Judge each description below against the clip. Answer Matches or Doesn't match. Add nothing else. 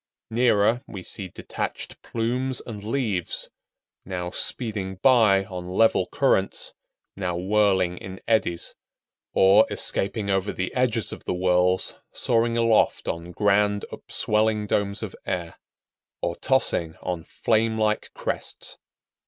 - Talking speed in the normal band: Doesn't match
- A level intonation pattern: Doesn't match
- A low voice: Matches